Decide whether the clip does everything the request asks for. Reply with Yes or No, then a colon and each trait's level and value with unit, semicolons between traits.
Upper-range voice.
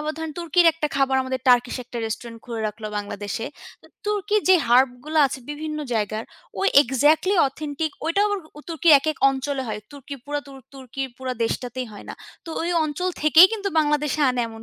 Yes: very high, 280 Hz